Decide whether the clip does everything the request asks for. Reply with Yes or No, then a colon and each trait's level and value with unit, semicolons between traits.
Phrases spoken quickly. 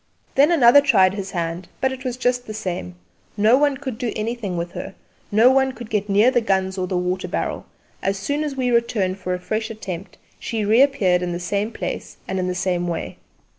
Yes: fast, 215 wpm